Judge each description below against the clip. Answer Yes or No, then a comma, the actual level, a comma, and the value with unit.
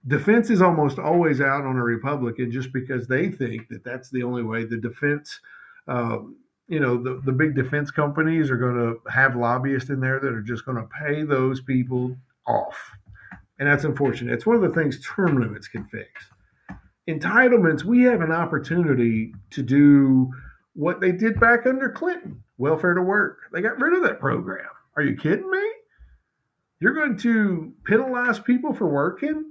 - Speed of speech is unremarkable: Yes, average, 180 wpm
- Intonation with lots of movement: Yes, wide, 7.7 semitones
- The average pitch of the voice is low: No, medium, 145 Hz